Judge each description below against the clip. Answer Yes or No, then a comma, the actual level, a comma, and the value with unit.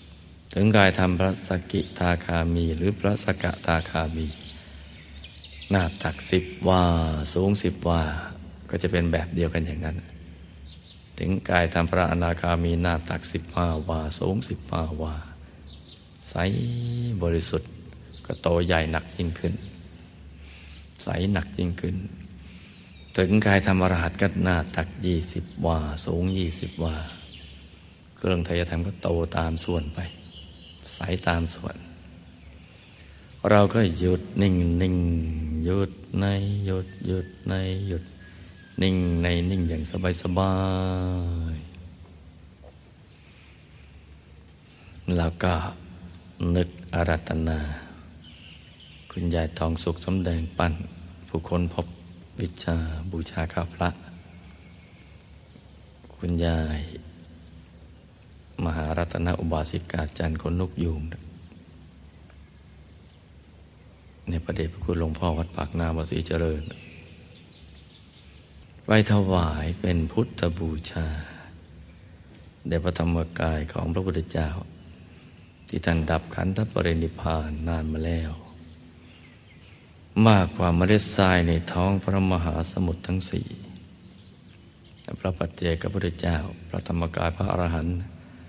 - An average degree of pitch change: No, narrow, 1.9 semitones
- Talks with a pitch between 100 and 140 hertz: No, very low, 85 Hz